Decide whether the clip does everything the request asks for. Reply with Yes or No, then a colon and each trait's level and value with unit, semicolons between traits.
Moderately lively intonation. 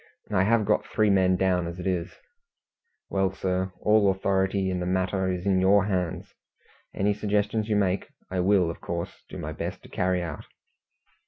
No: narrow, 1.7 semitones